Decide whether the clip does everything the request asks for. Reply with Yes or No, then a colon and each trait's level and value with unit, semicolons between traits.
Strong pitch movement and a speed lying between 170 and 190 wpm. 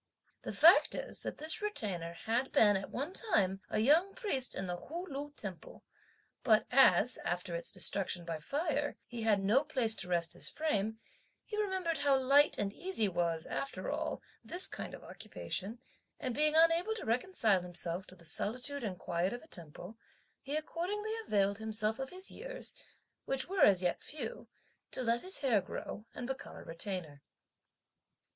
Yes: wide, 8.1 semitones; average, 175 wpm